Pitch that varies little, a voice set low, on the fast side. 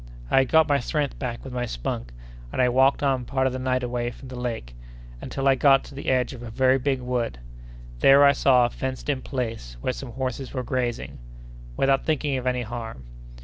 Yes: narrow, 1.9 semitones; low, 130 Hz; fast, 220 wpm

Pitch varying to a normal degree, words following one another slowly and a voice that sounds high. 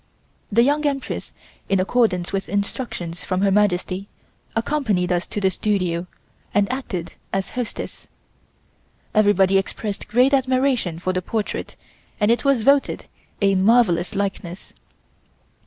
Yes: average, 4.5 semitones; slow, 125 wpm; high, 200 Hz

